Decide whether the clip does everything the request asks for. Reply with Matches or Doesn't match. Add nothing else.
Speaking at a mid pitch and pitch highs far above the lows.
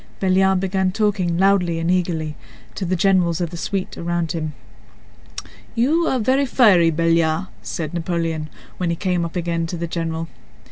Doesn't match